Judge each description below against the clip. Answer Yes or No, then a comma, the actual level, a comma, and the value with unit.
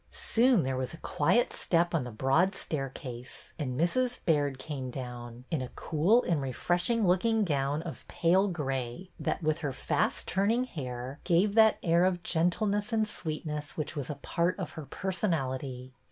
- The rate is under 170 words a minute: No, average, 175 wpm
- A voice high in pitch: No, medium, 160 Hz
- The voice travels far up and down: Yes, wide, 5.8 semitones